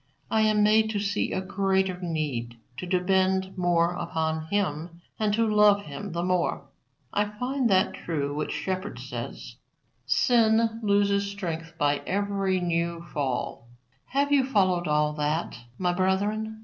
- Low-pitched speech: No, high, 190 Hz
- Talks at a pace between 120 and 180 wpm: Yes, average, 145 wpm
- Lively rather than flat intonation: No, average, 3.8 semitones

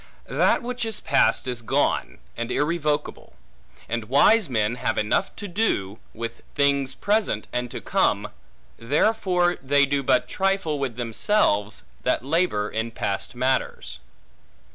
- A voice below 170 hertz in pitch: Yes, medium, 140 Hz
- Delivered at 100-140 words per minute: Yes, slow, 135 wpm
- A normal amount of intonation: No, wide, 7.6 semitones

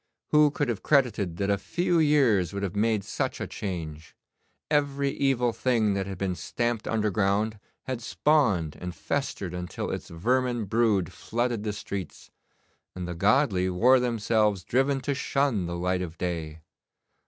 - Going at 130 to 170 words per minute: Yes, average, 155 wpm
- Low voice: Yes, low, 105 Hz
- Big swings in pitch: Yes, wide, 5.7 semitones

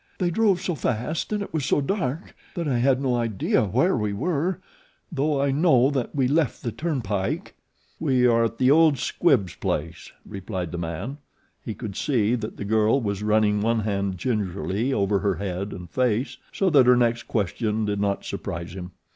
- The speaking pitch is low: Yes, low, 115 Hz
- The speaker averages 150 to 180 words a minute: No, average, 190 wpm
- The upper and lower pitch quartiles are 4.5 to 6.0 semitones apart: Yes, wide, 5.5 semitones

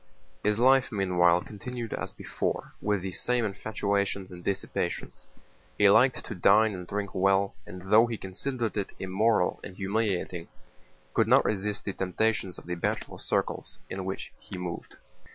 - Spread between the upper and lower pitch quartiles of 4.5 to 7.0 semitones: No, average, 2.8 semitones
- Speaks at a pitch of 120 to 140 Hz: No, low, 100 Hz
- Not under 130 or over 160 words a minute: Yes, average, 155 wpm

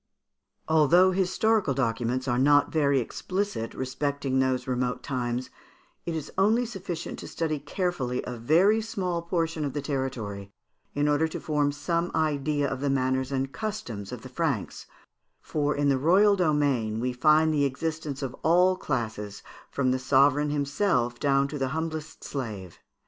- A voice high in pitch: No, medium, 145 Hz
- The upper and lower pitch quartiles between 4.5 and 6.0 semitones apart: No, average, 4.0 semitones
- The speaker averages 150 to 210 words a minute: Yes, average, 160 wpm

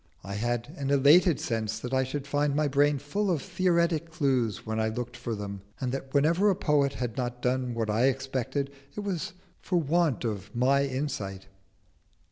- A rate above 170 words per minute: Yes, average, 185 wpm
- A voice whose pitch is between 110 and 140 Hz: Yes, low, 135 Hz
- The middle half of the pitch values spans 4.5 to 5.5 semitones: No, average, 3.8 semitones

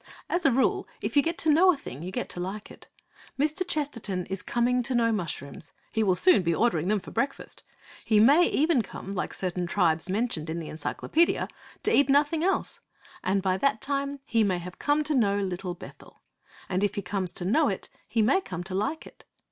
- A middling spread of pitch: No, wide, 7.7 semitones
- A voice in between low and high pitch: No, high, 215 Hz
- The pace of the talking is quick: Yes, fast, 215 wpm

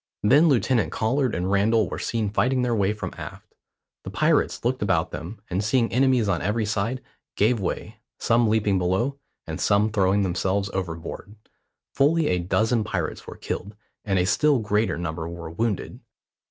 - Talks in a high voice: No, low, 105 Hz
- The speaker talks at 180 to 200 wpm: No, average, 165 wpm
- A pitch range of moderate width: Yes, average, 3.9 semitones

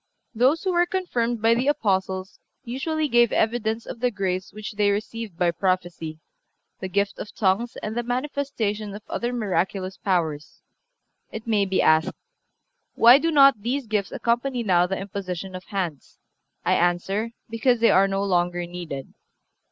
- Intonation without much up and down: No, average, 4.2 semitones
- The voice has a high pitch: Yes, high, 210 Hz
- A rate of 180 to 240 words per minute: No, average, 160 wpm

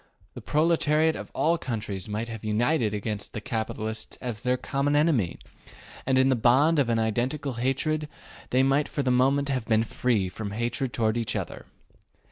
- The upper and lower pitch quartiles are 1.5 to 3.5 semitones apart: No, average, 4.2 semitones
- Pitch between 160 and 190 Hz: No, low, 125 Hz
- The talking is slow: No, average, 175 wpm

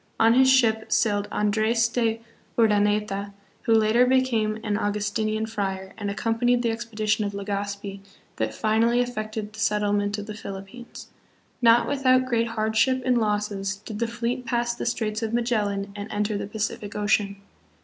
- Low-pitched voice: No, high, 215 Hz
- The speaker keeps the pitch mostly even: Yes, narrow, 2.2 semitones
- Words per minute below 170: Yes, average, 155 wpm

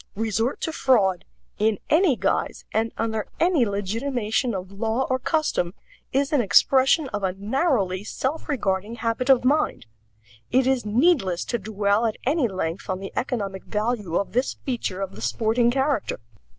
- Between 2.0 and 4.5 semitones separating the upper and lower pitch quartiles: No, average, 4.9 semitones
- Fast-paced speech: No, average, 160 wpm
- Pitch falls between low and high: No, high, 225 Hz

